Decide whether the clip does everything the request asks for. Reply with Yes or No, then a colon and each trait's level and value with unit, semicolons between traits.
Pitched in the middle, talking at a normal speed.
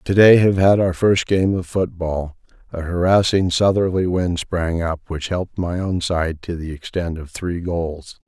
No: very low, 90 Hz; average, 190 wpm